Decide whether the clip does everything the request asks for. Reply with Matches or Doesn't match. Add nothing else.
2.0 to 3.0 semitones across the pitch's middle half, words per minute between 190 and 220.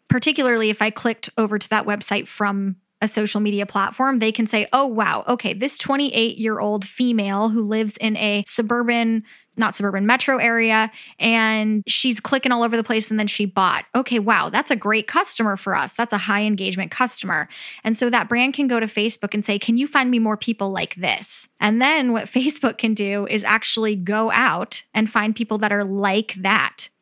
Matches